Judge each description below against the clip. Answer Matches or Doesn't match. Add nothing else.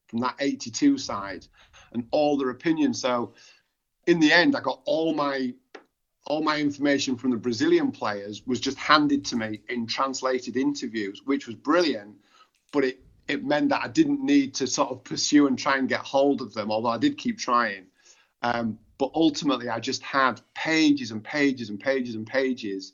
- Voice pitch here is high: Doesn't match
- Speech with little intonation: Doesn't match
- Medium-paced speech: Matches